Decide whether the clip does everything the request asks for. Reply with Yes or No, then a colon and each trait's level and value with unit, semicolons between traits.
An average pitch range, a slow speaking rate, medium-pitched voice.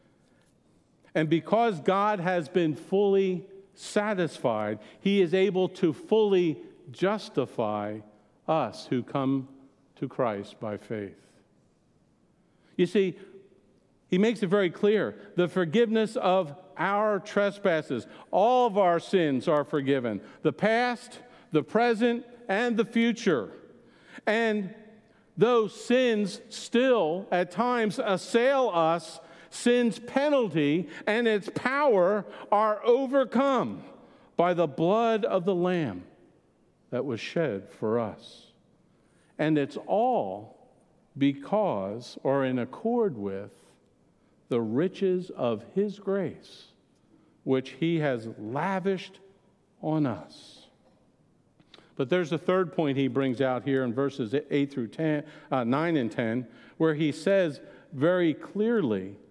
No: wide, 7.3 semitones; slow, 115 wpm; medium, 180 Hz